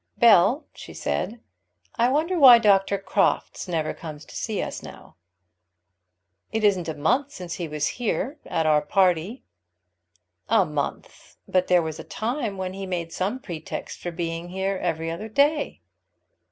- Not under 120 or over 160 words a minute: Yes, average, 155 wpm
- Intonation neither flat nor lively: No, wide, 5.7 semitones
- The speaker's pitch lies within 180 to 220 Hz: Yes, high, 190 Hz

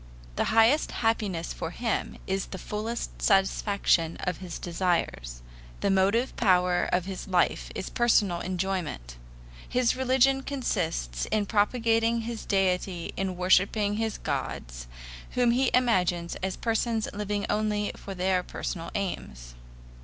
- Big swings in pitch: No, average, 4.0 semitones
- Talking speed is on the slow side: Yes, slow, 130 wpm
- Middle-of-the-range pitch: No, high, 195 Hz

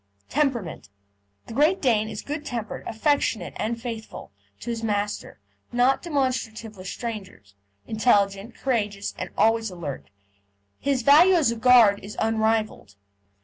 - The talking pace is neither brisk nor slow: No, slow, 130 wpm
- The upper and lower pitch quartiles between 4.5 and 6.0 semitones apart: No, average, 3.6 semitones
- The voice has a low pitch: No, high, 225 Hz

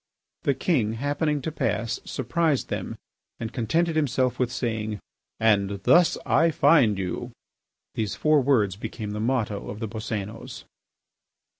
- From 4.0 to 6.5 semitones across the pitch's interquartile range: Yes, average, 5.1 semitones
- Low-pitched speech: Yes, low, 115 Hz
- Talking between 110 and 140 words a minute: Yes, slow, 135 wpm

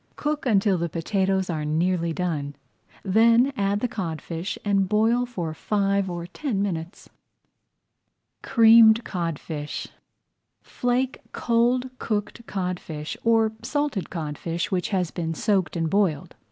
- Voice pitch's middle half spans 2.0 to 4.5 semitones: No, average, 5.1 semitones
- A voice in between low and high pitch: No, high, 195 Hz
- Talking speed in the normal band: No, slow, 120 wpm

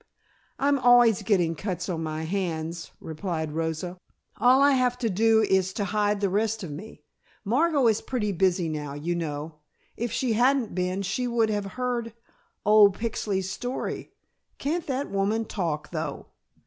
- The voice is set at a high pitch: Yes, high, 200 Hz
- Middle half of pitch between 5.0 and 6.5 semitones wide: Yes, wide, 5.4 semitones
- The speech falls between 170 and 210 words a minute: No, average, 160 wpm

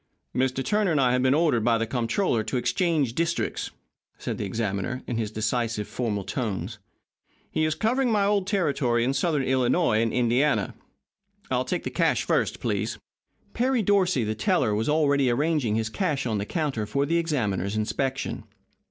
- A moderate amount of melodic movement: No, wide, 6.0 semitones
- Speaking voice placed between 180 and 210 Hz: No, low, 130 Hz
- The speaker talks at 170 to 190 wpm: Yes, average, 175 wpm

